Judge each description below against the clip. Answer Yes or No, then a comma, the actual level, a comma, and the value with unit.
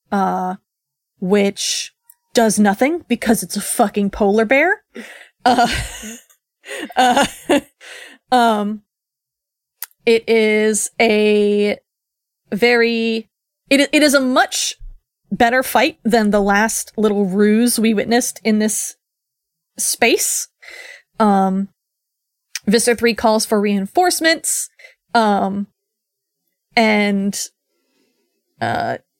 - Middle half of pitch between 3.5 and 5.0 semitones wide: Yes, average, 4.0 semitones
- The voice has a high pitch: Yes, high, 225 Hz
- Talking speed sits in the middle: No, slow, 90 wpm